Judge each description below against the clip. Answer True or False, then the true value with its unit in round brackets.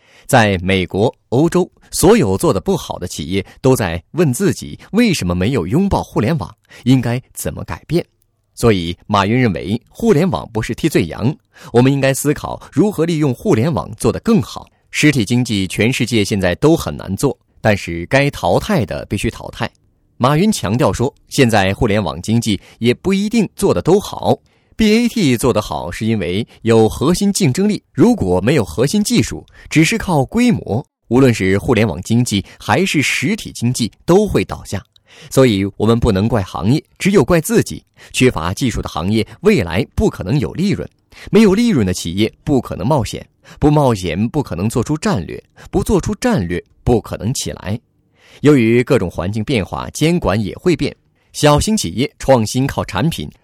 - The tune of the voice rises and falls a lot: True (7.0 semitones)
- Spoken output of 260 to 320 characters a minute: True (265 characters per minute)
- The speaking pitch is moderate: False (115 Hz)